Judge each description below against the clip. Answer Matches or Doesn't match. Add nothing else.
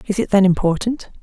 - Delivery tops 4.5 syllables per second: Matches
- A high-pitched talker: Matches